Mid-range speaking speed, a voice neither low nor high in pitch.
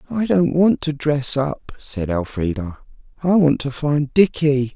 Yes: average, 165 wpm; medium, 145 Hz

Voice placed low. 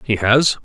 Yes: low, 115 Hz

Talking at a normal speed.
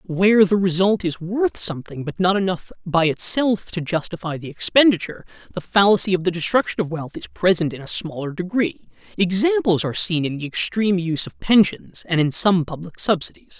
Yes: average, 185 wpm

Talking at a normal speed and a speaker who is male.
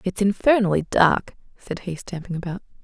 No: average, 150 wpm; female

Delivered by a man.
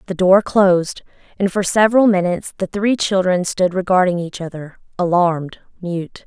No: female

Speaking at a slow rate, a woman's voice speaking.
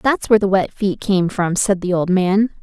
No: fast, 250 wpm; female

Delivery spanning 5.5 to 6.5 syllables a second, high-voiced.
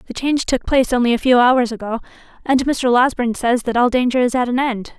Yes: 6.2 syllables/s; high, 245 Hz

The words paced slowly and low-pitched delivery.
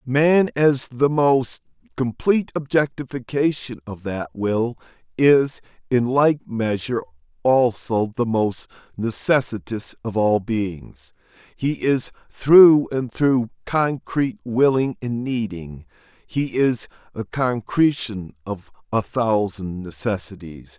Yes: slow, 105 wpm; low, 120 Hz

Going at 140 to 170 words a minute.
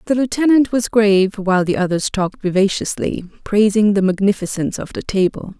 Yes: average, 160 wpm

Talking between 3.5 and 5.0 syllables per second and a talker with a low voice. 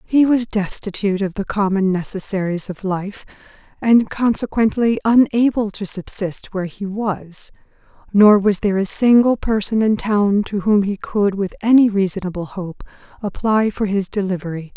No: 4.8 syllables/s; high, 205 Hz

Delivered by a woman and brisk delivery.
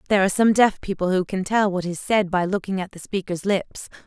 Yes: female; fast, 250 wpm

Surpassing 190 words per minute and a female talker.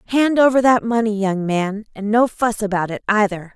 Yes: fast, 205 wpm; female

